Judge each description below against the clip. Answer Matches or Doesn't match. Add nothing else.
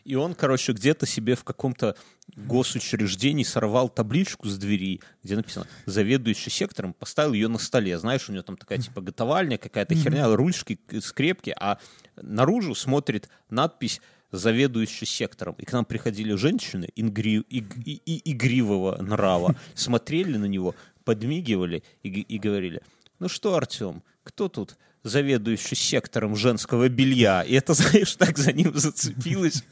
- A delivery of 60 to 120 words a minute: Doesn't match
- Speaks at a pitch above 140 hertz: Doesn't match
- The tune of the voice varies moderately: Matches